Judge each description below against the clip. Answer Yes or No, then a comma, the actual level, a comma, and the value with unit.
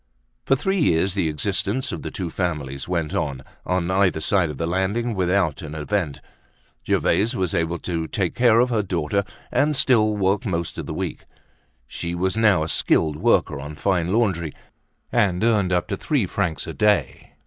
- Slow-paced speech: No, average, 180 wpm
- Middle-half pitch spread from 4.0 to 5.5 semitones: Yes, average, 4.4 semitones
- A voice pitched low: Yes, very low, 95 Hz